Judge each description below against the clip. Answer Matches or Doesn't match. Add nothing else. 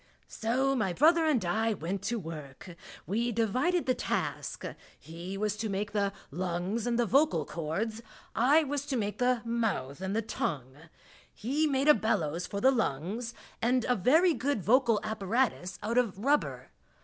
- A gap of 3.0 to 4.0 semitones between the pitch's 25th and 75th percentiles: Doesn't match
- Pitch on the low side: Doesn't match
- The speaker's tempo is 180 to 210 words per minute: Doesn't match